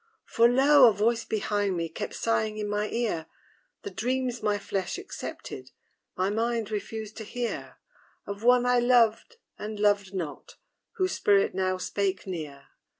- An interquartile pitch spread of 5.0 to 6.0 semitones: No, average, 3.2 semitones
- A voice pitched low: No, high, 215 Hz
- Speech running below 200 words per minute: Yes, average, 150 wpm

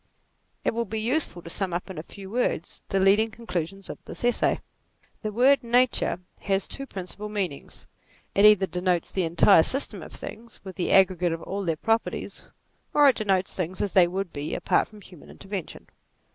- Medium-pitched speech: No, high, 195 Hz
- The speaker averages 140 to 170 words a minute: No, average, 185 wpm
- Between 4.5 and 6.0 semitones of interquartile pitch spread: No, average, 3.7 semitones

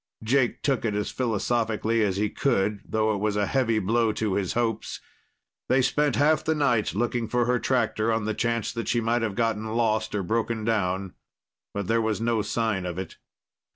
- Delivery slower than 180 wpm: No, average, 195 wpm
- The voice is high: No, low, 110 Hz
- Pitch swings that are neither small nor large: No, narrow, 2.1 semitones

